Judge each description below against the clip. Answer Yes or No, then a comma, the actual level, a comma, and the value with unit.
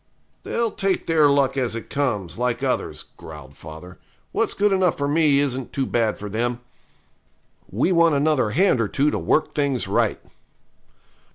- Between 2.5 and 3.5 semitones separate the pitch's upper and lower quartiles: No, average, 5.0 semitones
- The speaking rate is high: No, average, 165 wpm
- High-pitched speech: No, medium, 140 Hz